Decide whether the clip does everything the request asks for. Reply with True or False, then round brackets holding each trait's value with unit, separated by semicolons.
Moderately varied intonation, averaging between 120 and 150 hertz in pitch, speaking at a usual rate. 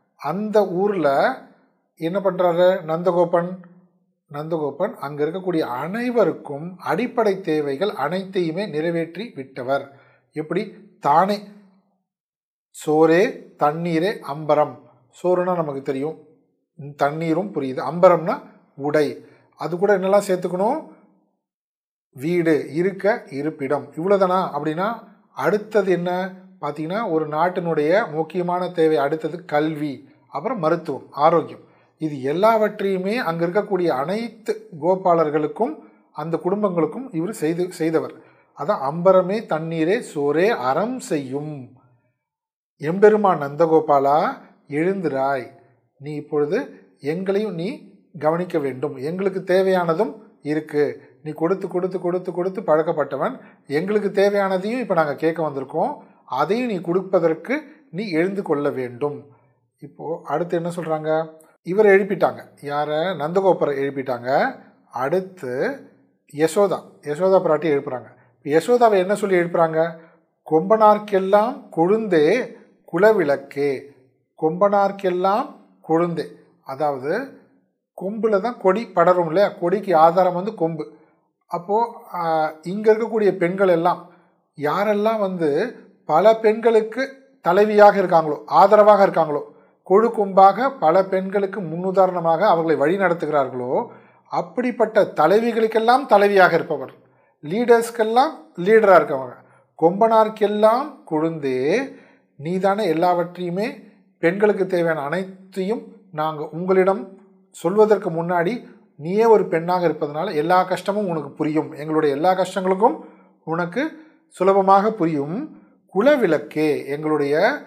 False (4.7 semitones; 180 Hz; 95 wpm)